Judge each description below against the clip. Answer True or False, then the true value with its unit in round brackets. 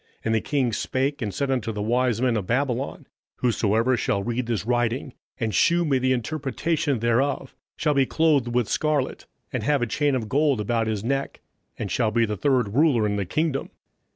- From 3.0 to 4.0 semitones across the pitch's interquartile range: True (3.7 semitones)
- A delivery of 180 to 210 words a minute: True (195 wpm)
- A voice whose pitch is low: True (125 Hz)